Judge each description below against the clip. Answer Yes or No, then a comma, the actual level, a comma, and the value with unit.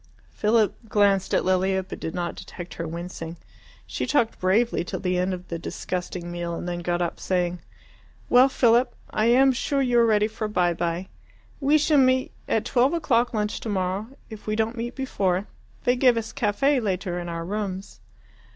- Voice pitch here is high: Yes, high, 205 Hz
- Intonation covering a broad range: No, average, 5.0 semitones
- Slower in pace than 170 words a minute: No, average, 185 wpm